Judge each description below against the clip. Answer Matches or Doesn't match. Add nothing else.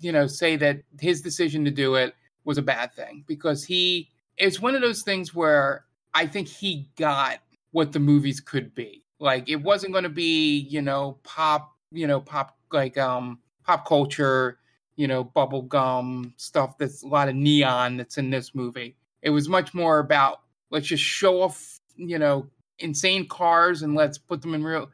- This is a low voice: Doesn't match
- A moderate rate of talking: Matches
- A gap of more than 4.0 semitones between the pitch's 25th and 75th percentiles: Doesn't match